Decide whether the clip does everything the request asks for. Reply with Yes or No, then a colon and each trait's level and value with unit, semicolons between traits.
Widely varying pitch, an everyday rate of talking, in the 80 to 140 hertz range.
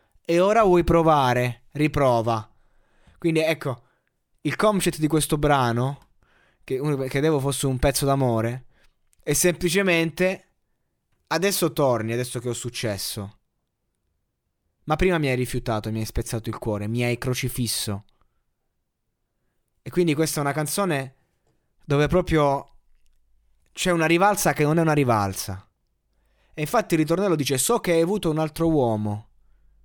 Yes: wide, 6.0 semitones; average, 135 wpm; low, 135 Hz